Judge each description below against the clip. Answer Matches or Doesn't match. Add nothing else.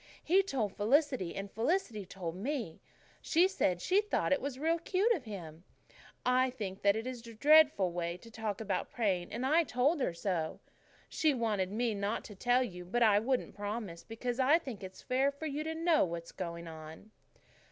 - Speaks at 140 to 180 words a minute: Doesn't match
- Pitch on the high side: Matches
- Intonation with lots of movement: Matches